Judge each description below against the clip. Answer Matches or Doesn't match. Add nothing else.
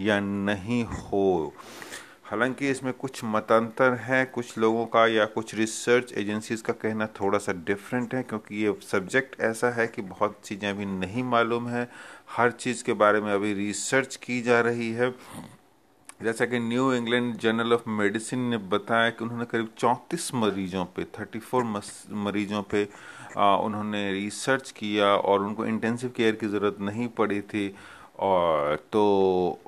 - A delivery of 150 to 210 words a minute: Matches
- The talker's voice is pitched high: Doesn't match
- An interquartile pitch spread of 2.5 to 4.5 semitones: Matches